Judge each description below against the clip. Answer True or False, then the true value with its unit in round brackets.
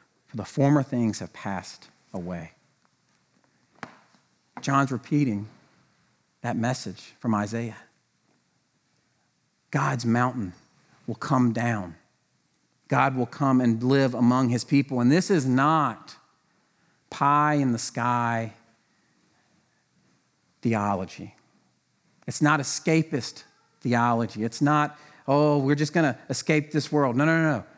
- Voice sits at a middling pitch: False (125 Hz)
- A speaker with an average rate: False (110 wpm)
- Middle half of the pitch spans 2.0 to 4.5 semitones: True (4.1 semitones)